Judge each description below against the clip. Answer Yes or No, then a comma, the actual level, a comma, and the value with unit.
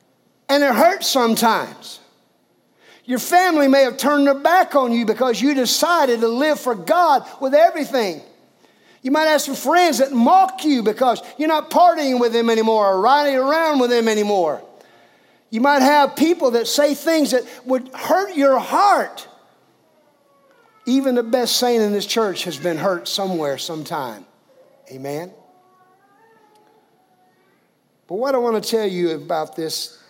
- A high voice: Yes, very high, 265 Hz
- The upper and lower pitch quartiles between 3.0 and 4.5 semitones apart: No, average, 5.0 semitones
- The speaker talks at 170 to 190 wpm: No, average, 155 wpm